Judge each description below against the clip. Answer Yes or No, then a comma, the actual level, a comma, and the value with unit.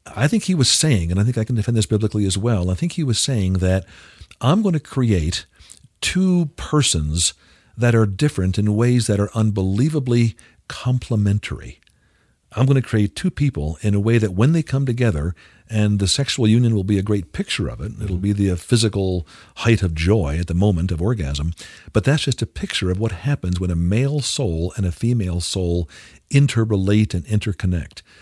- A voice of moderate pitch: No, low, 105 Hz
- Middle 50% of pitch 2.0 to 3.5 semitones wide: No, average, 4.6 semitones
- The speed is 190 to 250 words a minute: Yes, average, 195 wpm